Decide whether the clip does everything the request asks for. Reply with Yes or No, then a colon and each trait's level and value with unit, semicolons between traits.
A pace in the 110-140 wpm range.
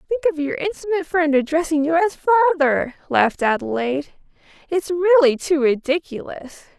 Yes: slow, 135 wpm